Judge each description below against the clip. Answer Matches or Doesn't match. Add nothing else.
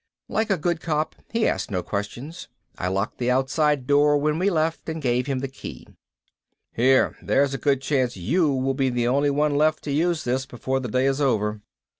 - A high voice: Doesn't match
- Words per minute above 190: Matches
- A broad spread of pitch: Doesn't match